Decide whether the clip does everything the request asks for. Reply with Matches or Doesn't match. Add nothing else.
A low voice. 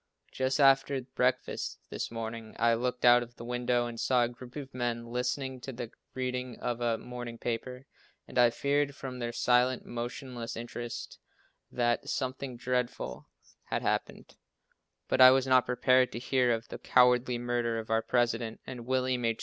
Matches